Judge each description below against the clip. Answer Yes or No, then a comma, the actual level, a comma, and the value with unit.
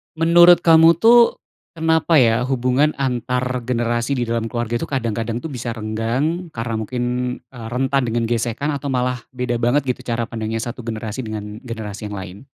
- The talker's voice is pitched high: No, low, 120 Hz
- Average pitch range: Yes, average, 3.0 semitones